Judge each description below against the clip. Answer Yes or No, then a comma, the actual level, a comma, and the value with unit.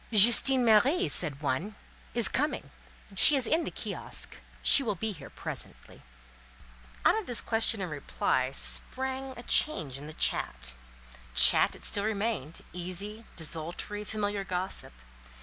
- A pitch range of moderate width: No, wide, 7.5 semitones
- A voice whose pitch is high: Yes, high, 200 Hz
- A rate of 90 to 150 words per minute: Yes, slow, 135 wpm